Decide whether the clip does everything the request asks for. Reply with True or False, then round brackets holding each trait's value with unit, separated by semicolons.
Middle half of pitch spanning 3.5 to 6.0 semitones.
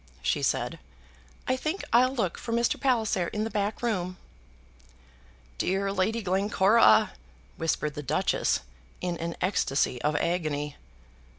True (5.1 semitones)